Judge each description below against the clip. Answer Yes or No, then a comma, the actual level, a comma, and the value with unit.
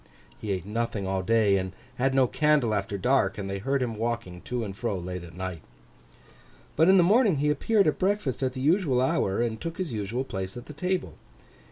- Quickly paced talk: Yes, fast, 215 wpm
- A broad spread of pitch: Yes, wide, 7.2 semitones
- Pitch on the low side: Yes, low, 120 Hz